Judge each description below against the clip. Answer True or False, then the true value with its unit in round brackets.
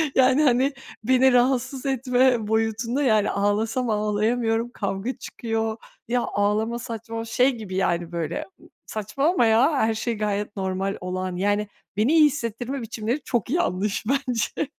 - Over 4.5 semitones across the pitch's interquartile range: False (3.4 semitones)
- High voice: True (225 Hz)